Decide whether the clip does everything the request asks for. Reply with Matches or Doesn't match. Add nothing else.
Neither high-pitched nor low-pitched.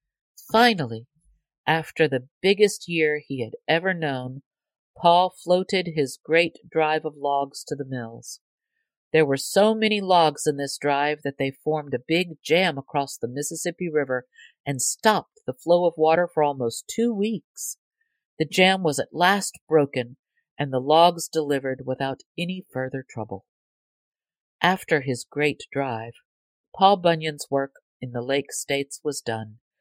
Matches